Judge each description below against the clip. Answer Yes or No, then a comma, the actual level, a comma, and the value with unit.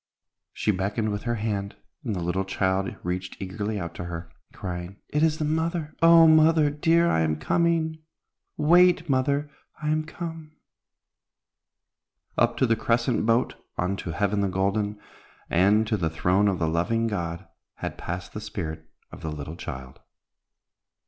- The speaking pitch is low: Yes, low, 105 Hz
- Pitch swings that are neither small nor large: No, wide, 8.9 semitones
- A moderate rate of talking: Yes, average, 160 wpm